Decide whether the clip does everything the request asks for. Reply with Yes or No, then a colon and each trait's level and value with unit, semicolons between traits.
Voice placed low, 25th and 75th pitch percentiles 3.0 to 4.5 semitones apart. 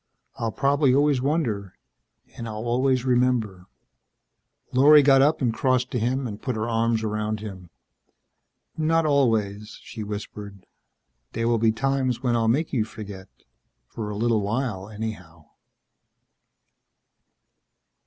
Yes: low, 115 Hz; average, 3.7 semitones